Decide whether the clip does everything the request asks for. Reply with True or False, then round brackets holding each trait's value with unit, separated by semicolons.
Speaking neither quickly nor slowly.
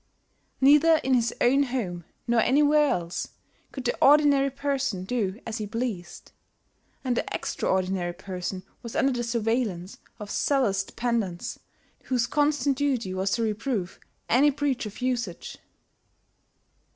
False (130 wpm)